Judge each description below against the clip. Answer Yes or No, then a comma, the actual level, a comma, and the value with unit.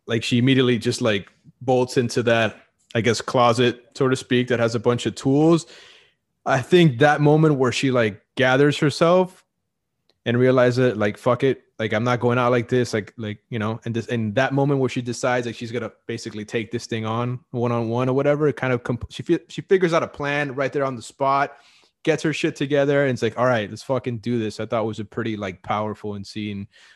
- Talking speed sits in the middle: No, fast, 235 wpm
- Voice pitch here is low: Yes, low, 125 Hz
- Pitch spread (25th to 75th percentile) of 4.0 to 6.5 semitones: No, average, 3.2 semitones